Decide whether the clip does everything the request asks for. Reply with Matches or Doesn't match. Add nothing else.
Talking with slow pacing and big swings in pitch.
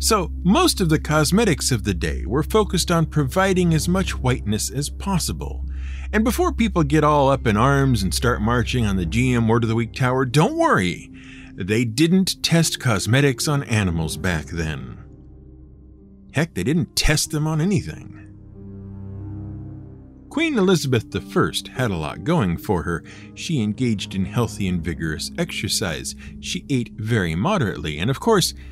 Doesn't match